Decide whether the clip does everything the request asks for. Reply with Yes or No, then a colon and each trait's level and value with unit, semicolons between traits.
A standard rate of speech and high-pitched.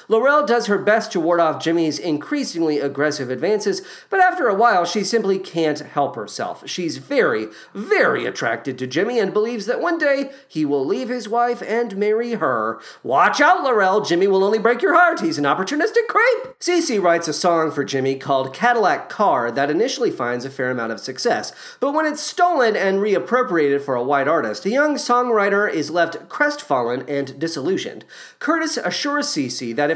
Yes: average, 185 wpm; high, 210 Hz